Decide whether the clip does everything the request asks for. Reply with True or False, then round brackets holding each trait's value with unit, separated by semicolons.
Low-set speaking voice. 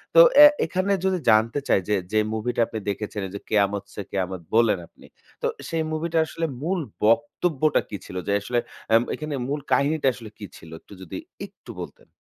True (115 Hz)